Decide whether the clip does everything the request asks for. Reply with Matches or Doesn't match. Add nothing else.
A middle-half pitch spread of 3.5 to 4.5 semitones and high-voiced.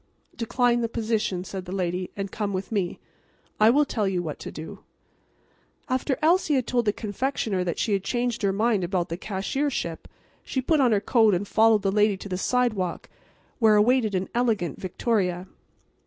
Matches